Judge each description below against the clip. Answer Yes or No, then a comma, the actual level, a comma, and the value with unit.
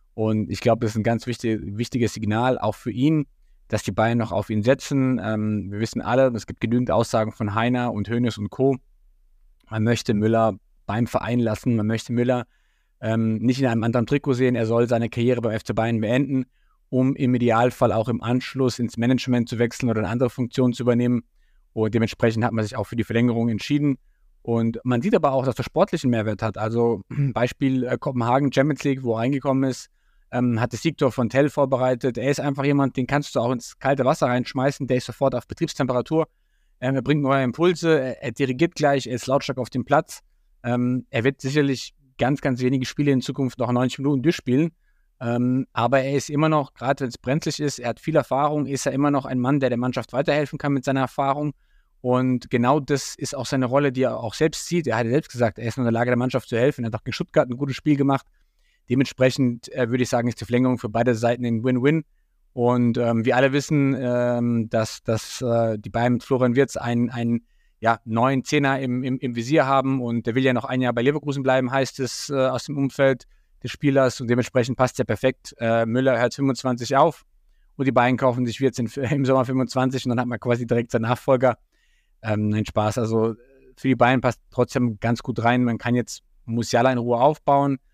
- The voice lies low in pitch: Yes, low, 125 Hz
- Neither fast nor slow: No, fast, 220 wpm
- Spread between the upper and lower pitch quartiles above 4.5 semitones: No, narrow, 2.5 semitones